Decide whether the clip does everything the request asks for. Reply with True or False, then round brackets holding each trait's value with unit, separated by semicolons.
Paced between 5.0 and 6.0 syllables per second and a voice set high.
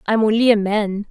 True (5.1 syllables/s; 210 Hz)